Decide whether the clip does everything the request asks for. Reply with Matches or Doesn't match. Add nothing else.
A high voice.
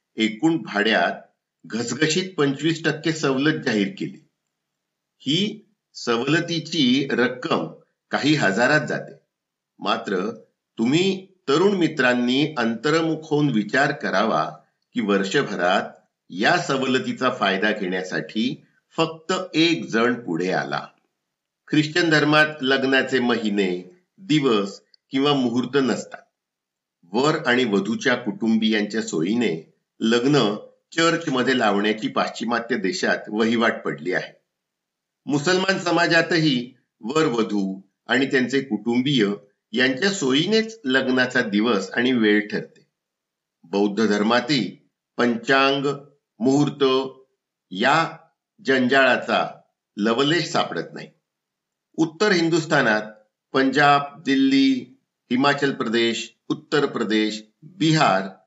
Doesn't match